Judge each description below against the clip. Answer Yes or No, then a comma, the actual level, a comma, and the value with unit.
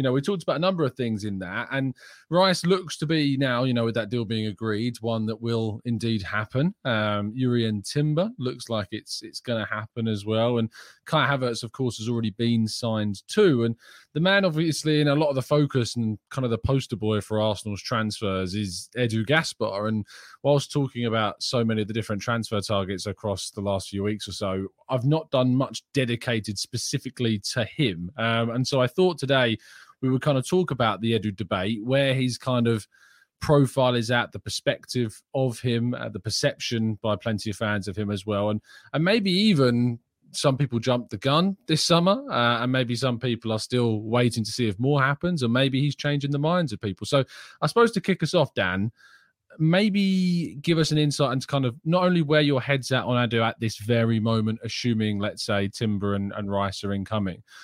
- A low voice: Yes, low, 120 Hz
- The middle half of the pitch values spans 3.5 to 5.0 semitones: Yes, average, 4.6 semitones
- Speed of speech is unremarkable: No, fast, 215 wpm